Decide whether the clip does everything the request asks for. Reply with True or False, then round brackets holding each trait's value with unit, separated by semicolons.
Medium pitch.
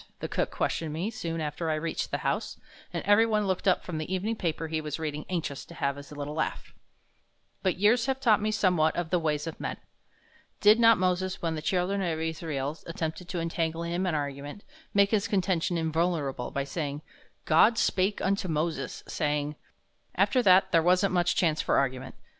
True (170 Hz)